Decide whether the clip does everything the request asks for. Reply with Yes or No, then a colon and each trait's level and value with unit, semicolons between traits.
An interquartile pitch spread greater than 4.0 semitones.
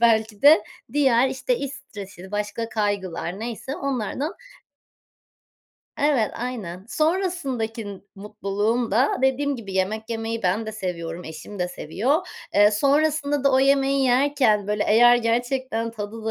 Yes: average, 4.6 semitones